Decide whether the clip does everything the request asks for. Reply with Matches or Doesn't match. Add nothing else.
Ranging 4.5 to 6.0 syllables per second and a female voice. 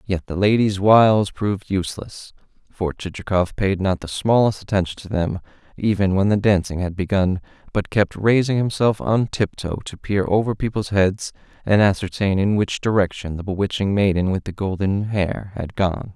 Doesn't match